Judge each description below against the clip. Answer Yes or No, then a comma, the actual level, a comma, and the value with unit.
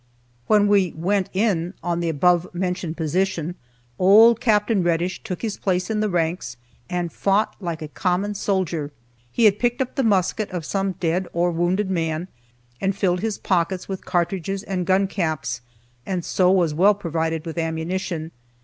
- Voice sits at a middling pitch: Yes, medium, 180 Hz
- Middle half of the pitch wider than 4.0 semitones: No, average, 2.7 semitones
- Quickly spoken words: No, average, 165 wpm